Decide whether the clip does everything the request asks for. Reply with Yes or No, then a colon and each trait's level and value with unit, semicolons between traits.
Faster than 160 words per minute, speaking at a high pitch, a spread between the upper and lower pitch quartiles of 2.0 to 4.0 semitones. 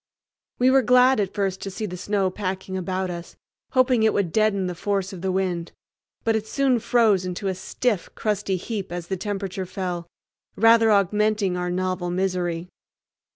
Yes: average, 175 wpm; high, 195 Hz; average, 2.9 semitones